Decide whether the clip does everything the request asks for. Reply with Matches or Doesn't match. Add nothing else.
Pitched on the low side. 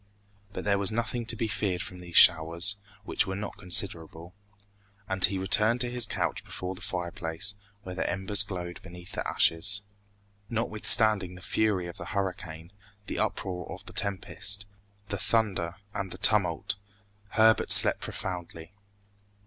Matches